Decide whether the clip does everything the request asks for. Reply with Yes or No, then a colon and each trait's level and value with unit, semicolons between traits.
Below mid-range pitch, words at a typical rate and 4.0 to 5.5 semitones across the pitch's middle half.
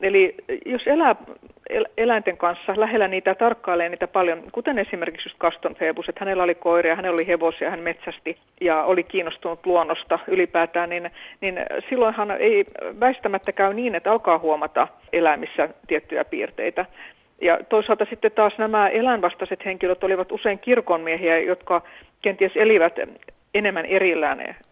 No: high, 190 Hz; average, 140 wpm; average, 4.4 semitones